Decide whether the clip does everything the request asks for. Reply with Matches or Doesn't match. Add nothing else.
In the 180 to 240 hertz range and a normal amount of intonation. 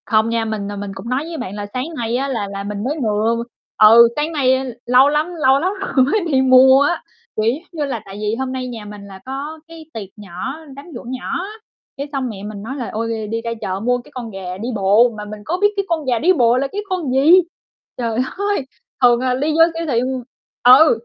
Doesn't match